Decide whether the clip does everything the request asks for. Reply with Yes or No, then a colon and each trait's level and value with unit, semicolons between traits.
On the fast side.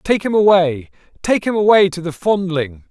No: average, 185 wpm